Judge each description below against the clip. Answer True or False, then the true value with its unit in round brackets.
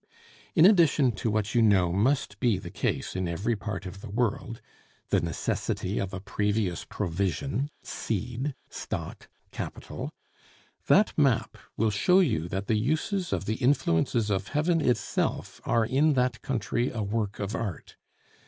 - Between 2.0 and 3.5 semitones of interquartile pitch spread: False (4.7 semitones)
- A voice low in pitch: True (110 Hz)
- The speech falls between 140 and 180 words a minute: True (155 wpm)